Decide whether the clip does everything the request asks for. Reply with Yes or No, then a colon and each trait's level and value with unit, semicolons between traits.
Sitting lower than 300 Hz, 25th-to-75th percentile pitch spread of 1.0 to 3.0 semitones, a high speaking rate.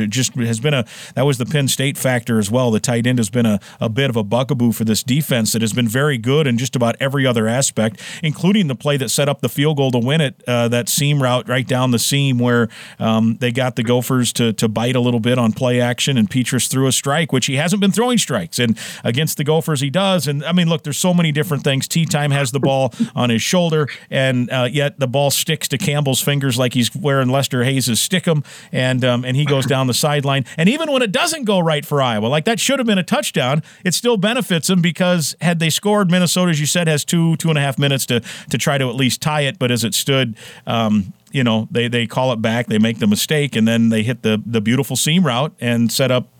No: low, 135 Hz; average, 4.3 semitones; fast, 260 wpm